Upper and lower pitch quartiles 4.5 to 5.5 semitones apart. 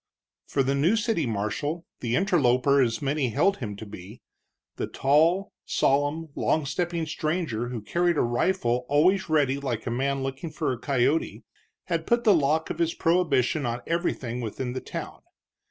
Yes: average, 5.1 semitones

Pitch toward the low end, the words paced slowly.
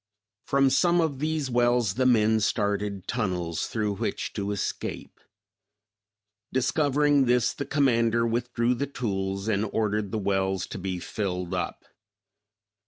Yes: low, 115 Hz; slow, 130 wpm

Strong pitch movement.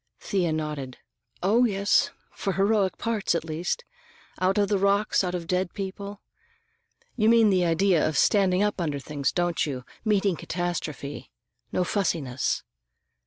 No: average, 3.7 semitones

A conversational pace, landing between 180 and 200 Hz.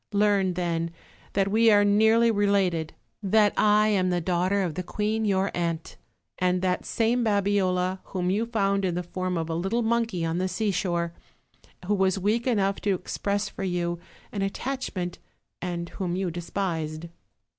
Yes: average, 165 wpm; high, 190 Hz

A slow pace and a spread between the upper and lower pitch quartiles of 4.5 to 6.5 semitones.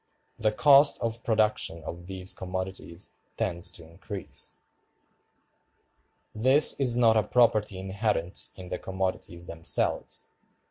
No: slow, 110 wpm; average, 3.8 semitones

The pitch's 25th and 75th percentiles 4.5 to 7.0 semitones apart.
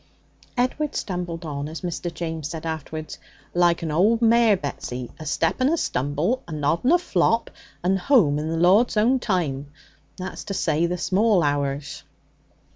Yes: wide, 5.6 semitones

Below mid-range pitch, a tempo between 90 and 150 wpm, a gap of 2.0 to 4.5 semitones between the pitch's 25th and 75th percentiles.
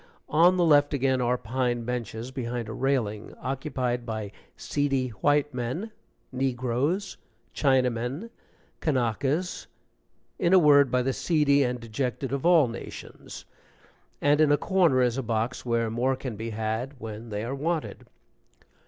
Yes: low, 130 Hz; average, 145 wpm; average, 3.5 semitones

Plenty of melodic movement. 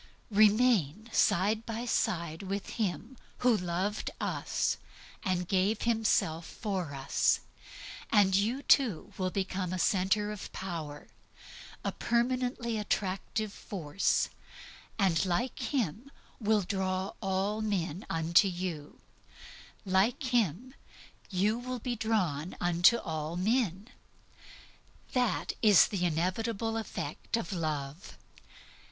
No: average, 4.2 semitones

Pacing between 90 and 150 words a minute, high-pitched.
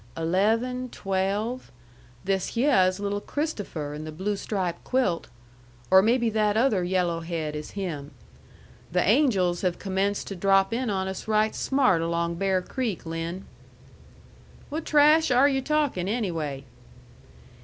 Yes: average, 140 wpm; high, 195 Hz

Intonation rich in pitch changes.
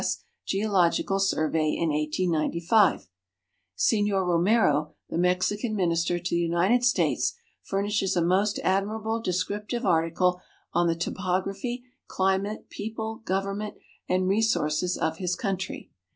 No: average, 3.3 semitones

